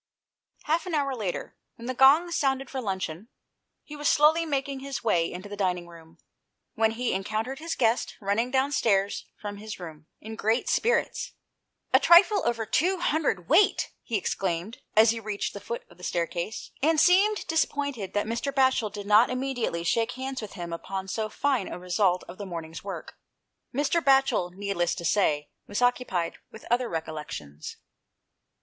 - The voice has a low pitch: No, high, 220 Hz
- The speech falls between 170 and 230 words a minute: Yes, average, 175 wpm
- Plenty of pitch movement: Yes, wide, 6.4 semitones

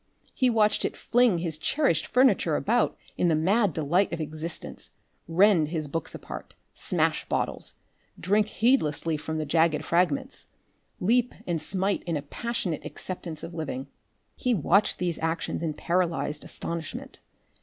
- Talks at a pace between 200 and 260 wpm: No, average, 145 wpm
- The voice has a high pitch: No, medium, 170 Hz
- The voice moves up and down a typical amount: Yes, average, 4.9 semitones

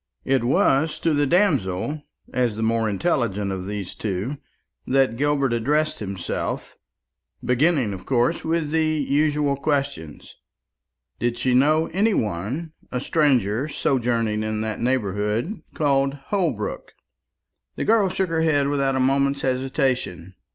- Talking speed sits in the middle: No, slow, 130 wpm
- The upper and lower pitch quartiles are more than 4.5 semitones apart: Yes, average, 5.3 semitones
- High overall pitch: No, low, 135 Hz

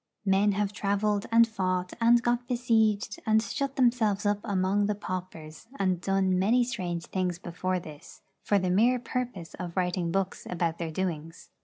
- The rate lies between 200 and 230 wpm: No, average, 165 wpm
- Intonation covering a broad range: No, average, 3.5 semitones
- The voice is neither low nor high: No, high, 195 Hz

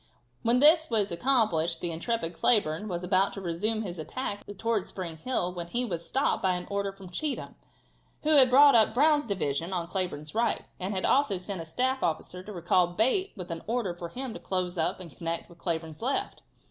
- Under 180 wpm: No, fast, 205 wpm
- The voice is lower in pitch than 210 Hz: Yes, high, 190 Hz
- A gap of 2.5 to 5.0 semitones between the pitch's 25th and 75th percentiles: No, wide, 5.5 semitones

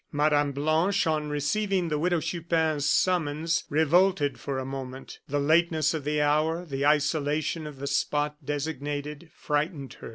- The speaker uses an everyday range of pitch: No, narrow, 1.9 semitones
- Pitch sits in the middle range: Yes, medium, 150 Hz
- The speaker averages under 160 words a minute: Yes, average, 150 wpm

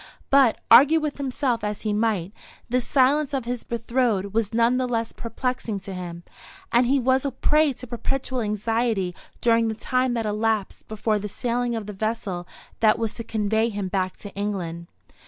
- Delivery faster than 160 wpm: Yes, average, 180 wpm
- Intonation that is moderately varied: Yes, average, 3.3 semitones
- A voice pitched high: Yes, high, 230 Hz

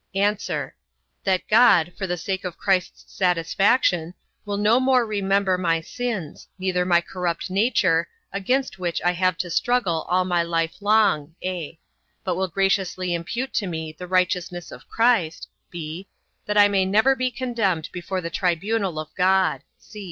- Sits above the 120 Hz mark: Yes, medium, 185 Hz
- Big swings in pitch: No, average, 3.1 semitones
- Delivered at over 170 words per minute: No, average, 155 wpm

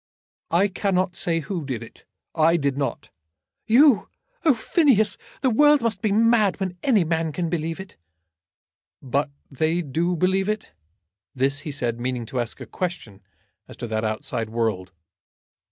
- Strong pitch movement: Yes, wide, 7.2 semitones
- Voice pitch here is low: No, medium, 170 Hz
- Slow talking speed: No, average, 155 wpm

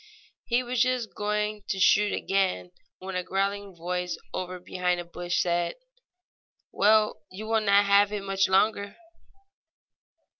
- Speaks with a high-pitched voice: Yes, high, 195 Hz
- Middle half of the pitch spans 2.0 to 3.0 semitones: Yes, narrow, 2.5 semitones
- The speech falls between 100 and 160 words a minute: Yes, average, 140 wpm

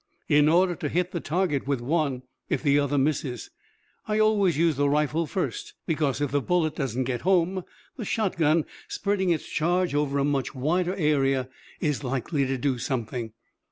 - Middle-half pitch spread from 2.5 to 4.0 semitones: No, average, 4.5 semitones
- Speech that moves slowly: No, average, 175 wpm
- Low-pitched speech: No, medium, 150 Hz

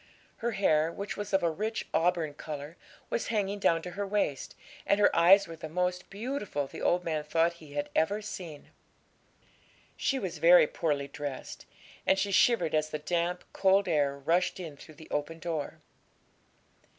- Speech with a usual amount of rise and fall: Yes, average, 4.2 semitones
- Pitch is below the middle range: No, medium, 170 Hz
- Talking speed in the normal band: Yes, average, 175 wpm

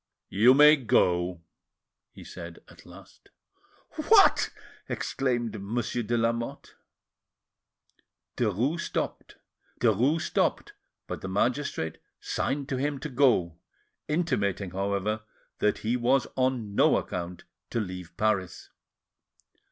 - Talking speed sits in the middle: No, slow, 100 wpm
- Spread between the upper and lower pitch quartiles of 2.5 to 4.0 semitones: No, average, 5.1 semitones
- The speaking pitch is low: Yes, low, 115 Hz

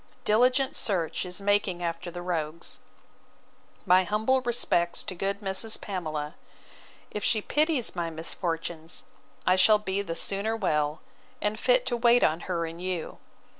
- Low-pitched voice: No, medium, 185 Hz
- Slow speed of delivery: No, average, 145 wpm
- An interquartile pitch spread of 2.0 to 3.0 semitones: No, average, 4.4 semitones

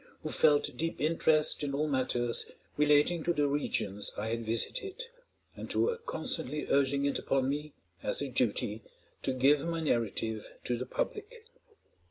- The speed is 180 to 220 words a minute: No, average, 160 wpm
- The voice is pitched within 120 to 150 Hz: Yes, medium, 140 Hz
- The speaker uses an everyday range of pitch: Yes, average, 4.0 semitones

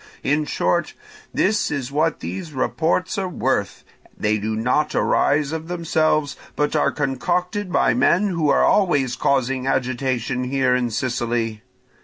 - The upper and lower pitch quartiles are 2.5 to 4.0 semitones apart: No, average, 4.4 semitones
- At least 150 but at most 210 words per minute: No, average, 140 wpm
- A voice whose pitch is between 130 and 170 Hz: Yes, medium, 140 Hz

